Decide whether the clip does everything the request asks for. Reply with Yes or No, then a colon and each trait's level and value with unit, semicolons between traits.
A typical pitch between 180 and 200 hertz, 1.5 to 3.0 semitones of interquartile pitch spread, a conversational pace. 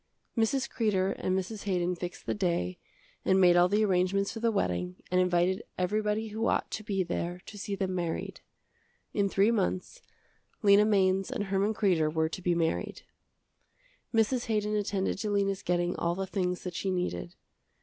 Yes: high, 190 Hz; average, 2.7 semitones; average, 175 wpm